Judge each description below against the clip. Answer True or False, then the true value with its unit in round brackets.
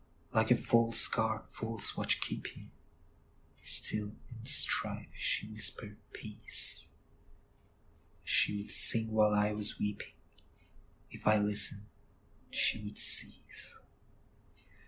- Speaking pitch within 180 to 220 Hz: False (105 Hz)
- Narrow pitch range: True (1.2 semitones)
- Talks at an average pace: False (95 wpm)